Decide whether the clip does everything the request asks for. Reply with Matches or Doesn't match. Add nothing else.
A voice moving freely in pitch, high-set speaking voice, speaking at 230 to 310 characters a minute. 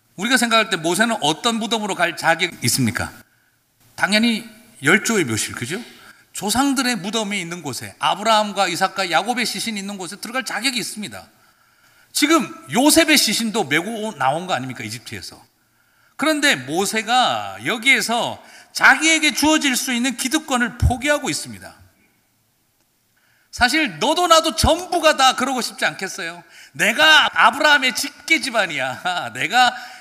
Doesn't match